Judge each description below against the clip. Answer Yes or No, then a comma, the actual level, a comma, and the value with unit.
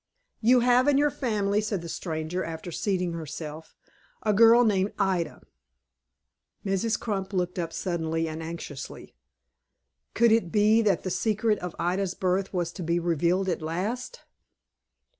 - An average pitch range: Yes, average, 4.2 semitones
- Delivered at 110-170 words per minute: Yes, average, 145 wpm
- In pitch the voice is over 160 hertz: Yes, medium, 185 Hz